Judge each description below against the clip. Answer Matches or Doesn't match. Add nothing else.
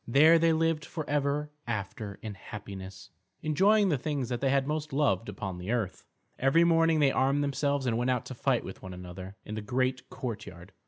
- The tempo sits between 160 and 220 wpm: Matches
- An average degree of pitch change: Doesn't match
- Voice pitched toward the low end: Matches